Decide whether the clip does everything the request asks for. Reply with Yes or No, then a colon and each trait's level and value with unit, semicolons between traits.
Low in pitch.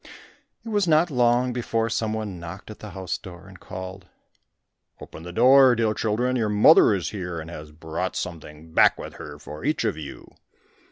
Yes: low, 100 Hz